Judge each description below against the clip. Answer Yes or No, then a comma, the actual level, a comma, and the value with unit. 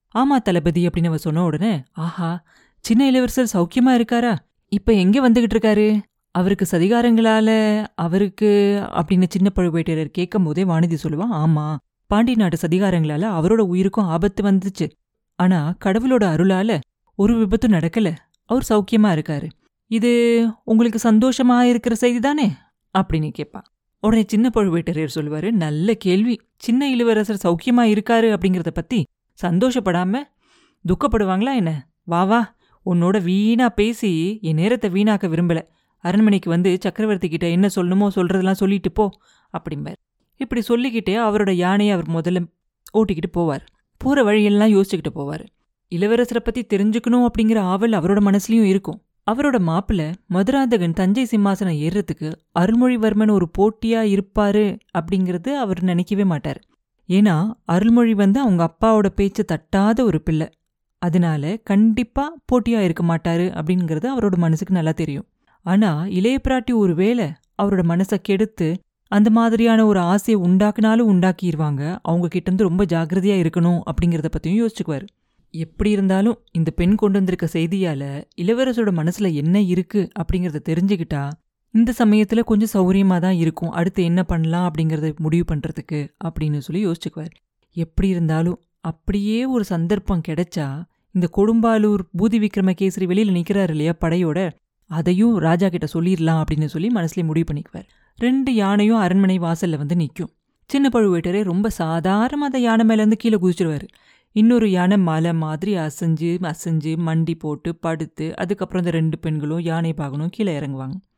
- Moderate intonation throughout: Yes, average, 4.5 semitones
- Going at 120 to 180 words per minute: Yes, fast, 130 wpm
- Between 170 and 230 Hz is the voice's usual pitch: Yes, high, 190 Hz